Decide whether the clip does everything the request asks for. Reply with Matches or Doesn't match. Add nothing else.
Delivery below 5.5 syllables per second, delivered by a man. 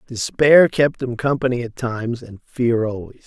Matches